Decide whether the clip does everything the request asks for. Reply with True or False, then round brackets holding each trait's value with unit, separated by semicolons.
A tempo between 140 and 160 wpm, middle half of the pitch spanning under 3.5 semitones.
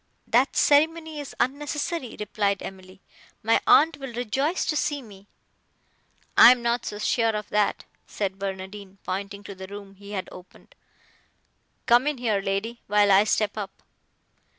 False (150 wpm; 4.5 semitones)